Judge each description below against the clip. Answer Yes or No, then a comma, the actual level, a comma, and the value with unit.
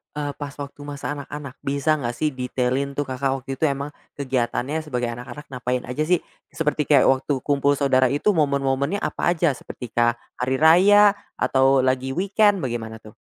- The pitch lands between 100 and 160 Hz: Yes, medium, 140 Hz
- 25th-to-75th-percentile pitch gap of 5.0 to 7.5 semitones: No, narrow, 2.5 semitones